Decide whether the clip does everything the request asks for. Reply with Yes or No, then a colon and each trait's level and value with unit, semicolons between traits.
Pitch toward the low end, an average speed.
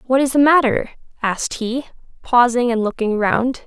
No: high, 245 Hz; average, 165 wpm